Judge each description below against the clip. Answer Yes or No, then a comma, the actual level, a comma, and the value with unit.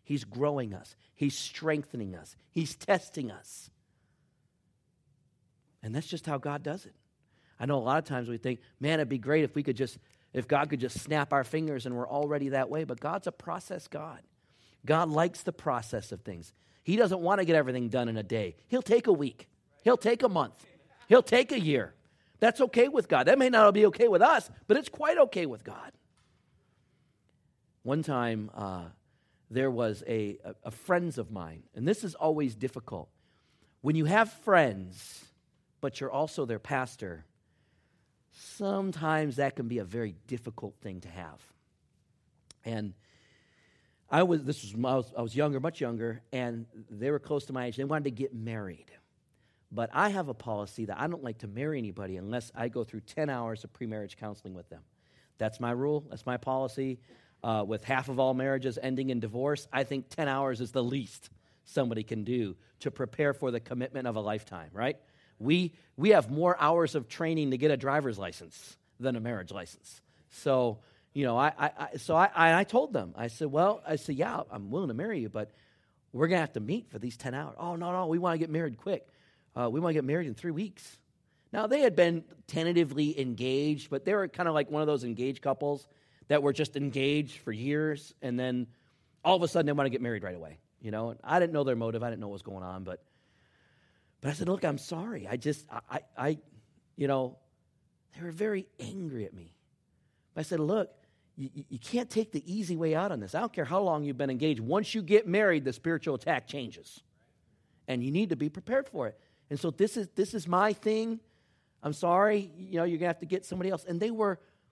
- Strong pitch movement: Yes, wide, 5.8 semitones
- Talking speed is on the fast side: Yes, fast, 210 wpm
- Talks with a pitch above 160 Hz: No, medium, 140 Hz